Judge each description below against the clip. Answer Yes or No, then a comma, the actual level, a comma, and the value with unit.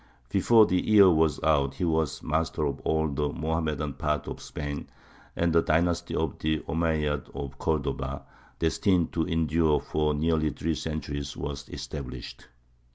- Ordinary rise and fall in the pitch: No, narrow, 2.1 semitones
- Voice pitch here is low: Yes, very low, 80 Hz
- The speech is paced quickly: No, average, 150 wpm